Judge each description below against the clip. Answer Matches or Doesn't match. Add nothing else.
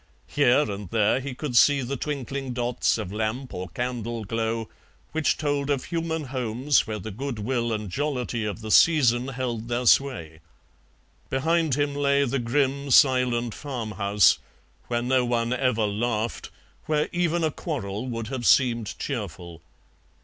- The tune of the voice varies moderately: Matches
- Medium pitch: Doesn't match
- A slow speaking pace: Doesn't match